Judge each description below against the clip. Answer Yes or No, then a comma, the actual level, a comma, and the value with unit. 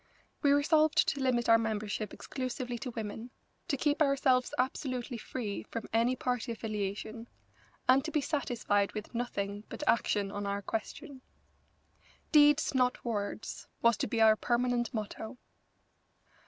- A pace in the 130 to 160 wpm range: Yes, average, 140 wpm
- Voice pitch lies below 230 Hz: No, high, 240 Hz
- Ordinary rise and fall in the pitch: Yes, average, 3.3 semitones